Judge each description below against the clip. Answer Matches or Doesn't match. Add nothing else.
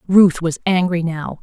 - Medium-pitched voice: Matches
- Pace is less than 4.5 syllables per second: Matches